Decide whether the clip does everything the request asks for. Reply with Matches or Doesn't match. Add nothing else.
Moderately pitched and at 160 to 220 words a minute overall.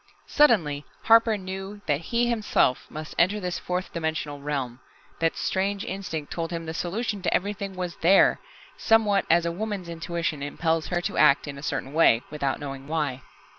Matches